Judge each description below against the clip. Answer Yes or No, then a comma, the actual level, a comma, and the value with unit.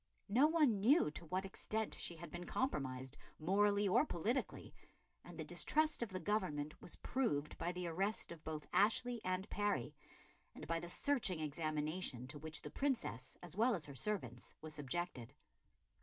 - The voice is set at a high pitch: No, medium, 180 Hz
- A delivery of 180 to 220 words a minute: No, average, 170 wpm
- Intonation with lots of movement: Yes, wide, 5.8 semitones